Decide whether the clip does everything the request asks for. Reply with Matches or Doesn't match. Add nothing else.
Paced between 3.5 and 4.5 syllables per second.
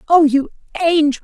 Doesn't match